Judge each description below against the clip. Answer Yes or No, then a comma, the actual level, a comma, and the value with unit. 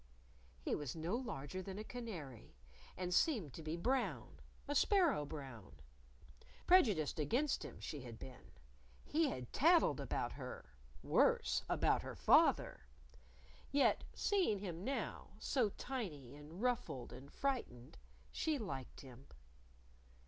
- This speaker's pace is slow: Yes, slow, 125 wpm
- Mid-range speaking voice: Yes, medium, 180 Hz